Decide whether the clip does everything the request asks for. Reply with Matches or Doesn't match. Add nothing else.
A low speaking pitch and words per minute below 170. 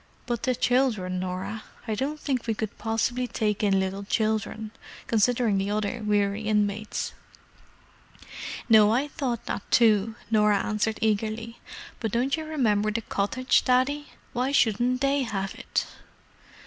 Doesn't match